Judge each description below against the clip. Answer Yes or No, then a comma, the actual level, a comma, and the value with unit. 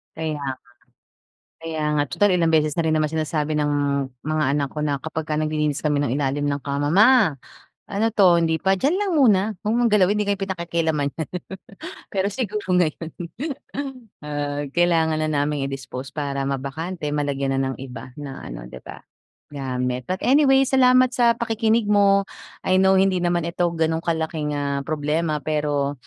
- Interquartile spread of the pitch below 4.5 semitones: No, average, 4.8 semitones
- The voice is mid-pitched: Yes, medium, 160 Hz